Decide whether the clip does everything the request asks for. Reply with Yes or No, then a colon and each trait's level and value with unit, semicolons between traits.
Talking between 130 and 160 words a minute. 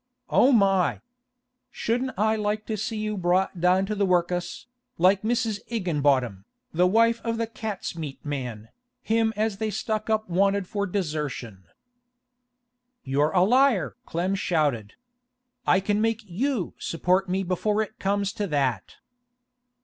Yes: average, 140 wpm